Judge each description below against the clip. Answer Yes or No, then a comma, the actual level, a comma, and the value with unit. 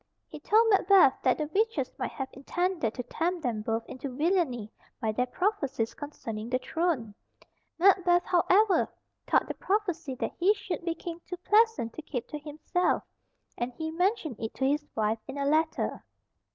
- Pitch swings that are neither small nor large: No, wide, 6.3 semitones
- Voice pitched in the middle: No, very high, 315 Hz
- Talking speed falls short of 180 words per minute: Yes, average, 170 wpm